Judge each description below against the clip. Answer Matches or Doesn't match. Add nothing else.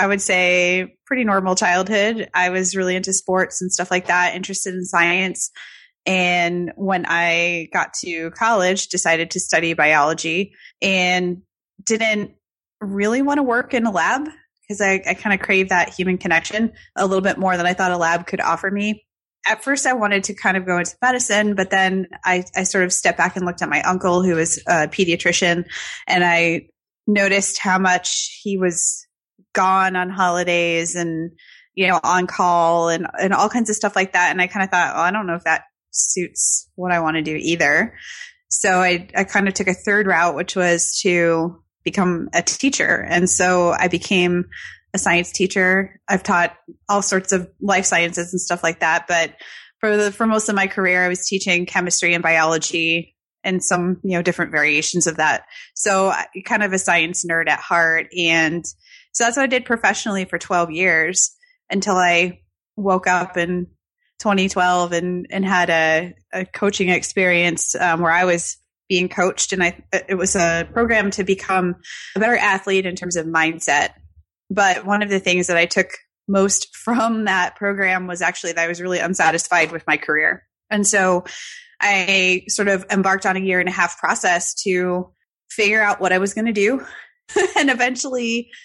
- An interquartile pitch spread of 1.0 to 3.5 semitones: Matches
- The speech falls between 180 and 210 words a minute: Matches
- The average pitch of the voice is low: Doesn't match